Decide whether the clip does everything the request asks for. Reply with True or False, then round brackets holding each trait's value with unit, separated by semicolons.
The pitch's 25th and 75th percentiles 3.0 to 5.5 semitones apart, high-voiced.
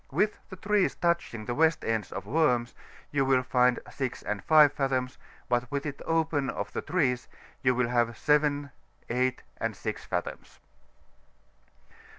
False (3.6 semitones; 135 Hz)